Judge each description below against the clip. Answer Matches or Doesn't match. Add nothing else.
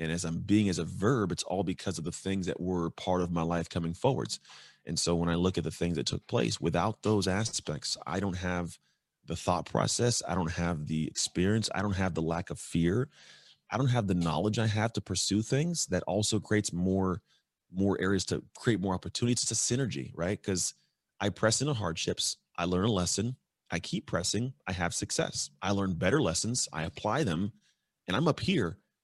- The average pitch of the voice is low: Matches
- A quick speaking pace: Matches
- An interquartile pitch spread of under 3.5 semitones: Doesn't match